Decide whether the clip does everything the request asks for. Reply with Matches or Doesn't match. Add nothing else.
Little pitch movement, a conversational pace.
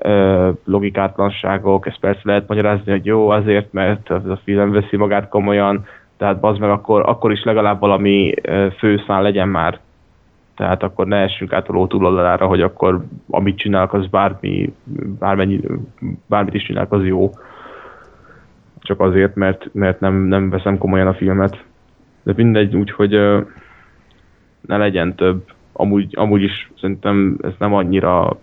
Matches